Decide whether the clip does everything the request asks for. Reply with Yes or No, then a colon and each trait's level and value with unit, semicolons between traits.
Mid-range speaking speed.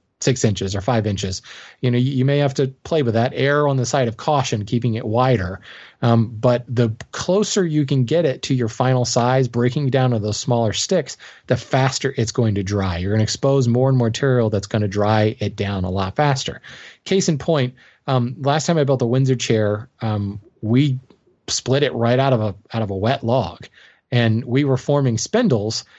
No: fast, 215 wpm